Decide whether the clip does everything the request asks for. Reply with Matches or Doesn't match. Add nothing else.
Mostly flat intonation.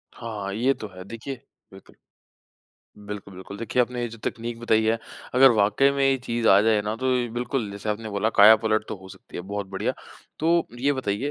Doesn't match